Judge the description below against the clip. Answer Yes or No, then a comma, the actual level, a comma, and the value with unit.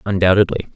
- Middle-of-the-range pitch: No, very low, 95 Hz